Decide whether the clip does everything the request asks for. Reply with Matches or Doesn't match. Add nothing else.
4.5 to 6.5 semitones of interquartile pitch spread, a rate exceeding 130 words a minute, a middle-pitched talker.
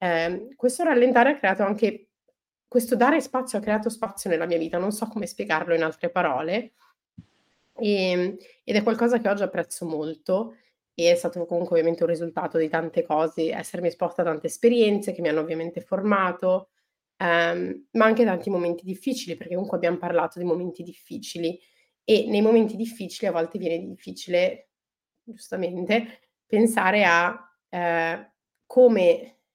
Matches